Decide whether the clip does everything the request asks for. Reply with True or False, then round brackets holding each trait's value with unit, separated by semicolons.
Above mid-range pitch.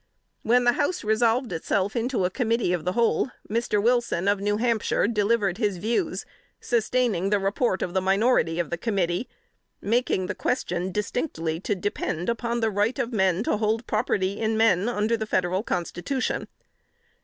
True (210 Hz)